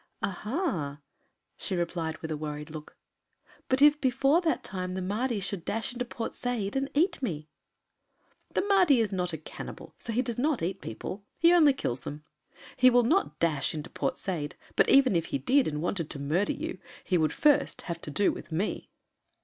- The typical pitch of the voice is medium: No, high, 200 Hz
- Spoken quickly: No, average, 195 wpm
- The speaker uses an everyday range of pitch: No, wide, 8.4 semitones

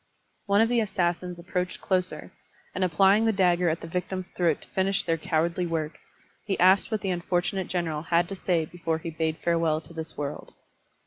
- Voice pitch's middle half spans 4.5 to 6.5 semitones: No, narrow, 2.5 semitones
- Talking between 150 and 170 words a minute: No, average, 190 wpm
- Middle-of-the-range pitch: Yes, medium, 175 Hz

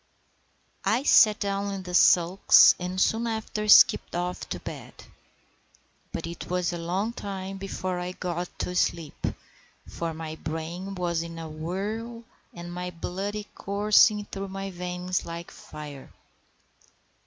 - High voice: No, medium, 180 Hz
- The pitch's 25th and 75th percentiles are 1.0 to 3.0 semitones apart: Yes, narrow, 2.6 semitones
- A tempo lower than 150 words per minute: Yes, average, 140 wpm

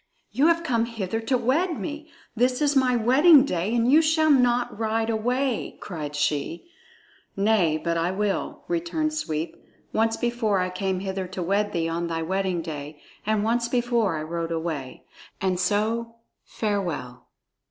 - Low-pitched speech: No, high, 215 Hz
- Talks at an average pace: Yes, average, 160 wpm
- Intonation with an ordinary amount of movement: No, wide, 6.2 semitones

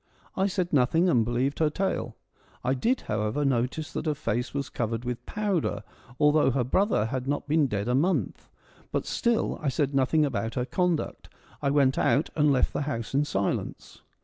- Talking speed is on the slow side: No, average, 195 wpm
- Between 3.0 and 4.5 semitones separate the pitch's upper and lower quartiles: Yes, average, 4.1 semitones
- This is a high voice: No, medium, 140 Hz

